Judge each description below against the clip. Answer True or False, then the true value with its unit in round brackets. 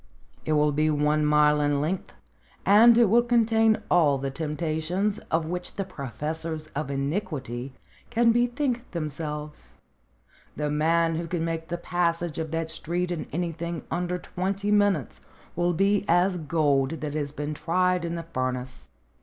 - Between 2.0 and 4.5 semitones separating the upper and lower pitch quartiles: True (3.4 semitones)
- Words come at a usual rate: True (155 wpm)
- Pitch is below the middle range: False (165 Hz)